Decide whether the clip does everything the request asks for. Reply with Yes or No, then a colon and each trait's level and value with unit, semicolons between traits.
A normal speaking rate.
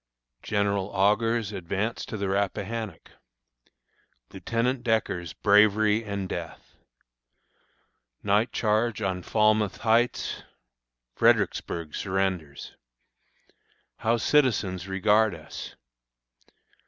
No: slow, 80 wpm